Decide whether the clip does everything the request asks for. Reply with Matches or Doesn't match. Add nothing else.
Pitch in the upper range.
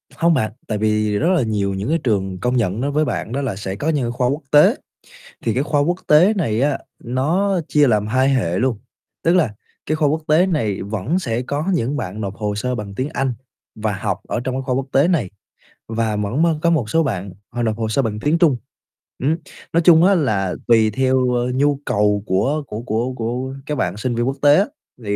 Doesn't match